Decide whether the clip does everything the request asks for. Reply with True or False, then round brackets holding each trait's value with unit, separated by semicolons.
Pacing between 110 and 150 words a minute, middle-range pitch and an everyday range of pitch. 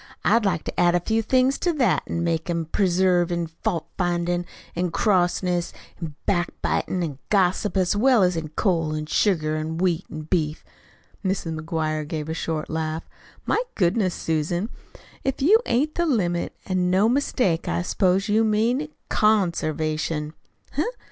False (160 wpm; 175 Hz; 4.2 semitones)